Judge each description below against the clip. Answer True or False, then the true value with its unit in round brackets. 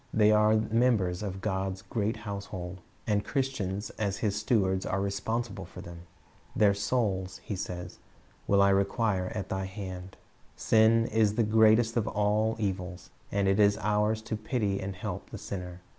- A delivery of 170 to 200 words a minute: False (160 wpm)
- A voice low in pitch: True (100 Hz)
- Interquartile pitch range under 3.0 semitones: True (2.4 semitones)